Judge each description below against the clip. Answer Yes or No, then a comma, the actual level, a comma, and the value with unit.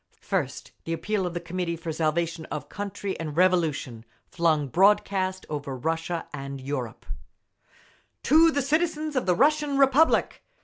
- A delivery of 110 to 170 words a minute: Yes, average, 140 wpm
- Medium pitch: Yes, medium, 175 Hz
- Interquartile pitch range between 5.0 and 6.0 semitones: Yes, wide, 5.5 semitones